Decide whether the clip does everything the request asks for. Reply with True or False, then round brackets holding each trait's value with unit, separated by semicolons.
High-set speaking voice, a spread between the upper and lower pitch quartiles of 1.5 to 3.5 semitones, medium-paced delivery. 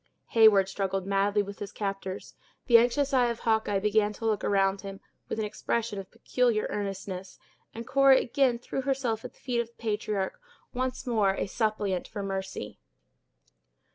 True (210 Hz; 3.1 semitones; 170 wpm)